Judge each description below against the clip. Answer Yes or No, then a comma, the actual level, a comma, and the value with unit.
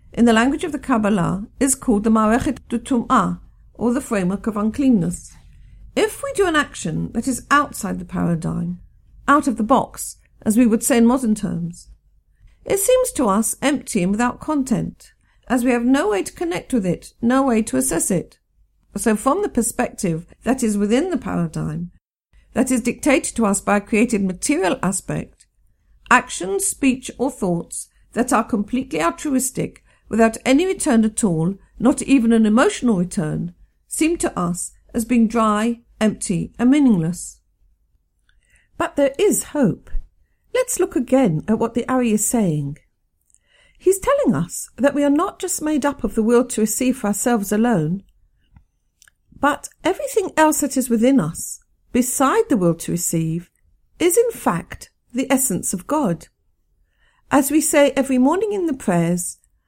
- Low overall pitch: No, high, 240 Hz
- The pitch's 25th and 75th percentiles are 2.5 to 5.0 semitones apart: No, wide, 5.4 semitones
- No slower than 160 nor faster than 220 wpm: Yes, average, 165 wpm